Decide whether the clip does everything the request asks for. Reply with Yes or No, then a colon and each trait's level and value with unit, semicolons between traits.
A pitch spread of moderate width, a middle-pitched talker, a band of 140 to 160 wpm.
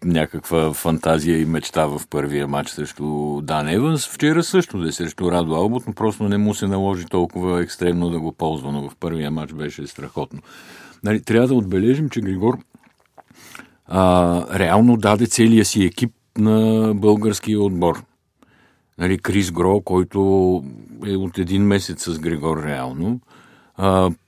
No: average, 4.8 semitones; very low, 90 Hz; average, 150 wpm